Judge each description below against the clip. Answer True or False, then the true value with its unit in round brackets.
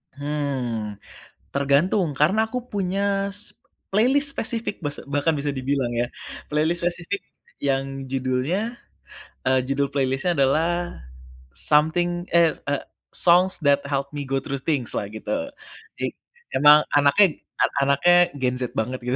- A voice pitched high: False (145 Hz)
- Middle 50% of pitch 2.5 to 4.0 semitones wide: False (4.6 semitones)